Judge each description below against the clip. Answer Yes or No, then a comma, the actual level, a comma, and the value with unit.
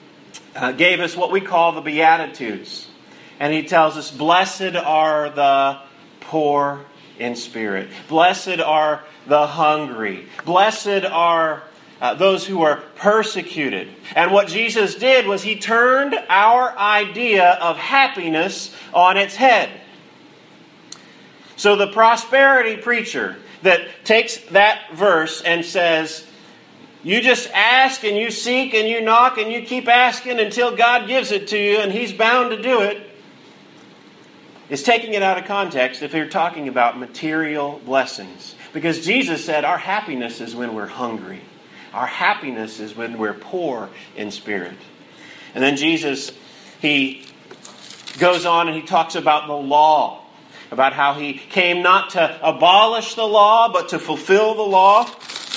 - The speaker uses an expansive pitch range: Yes, wide, 6.1 semitones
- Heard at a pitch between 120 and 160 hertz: No, medium, 175 Hz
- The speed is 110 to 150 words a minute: Yes, average, 140 wpm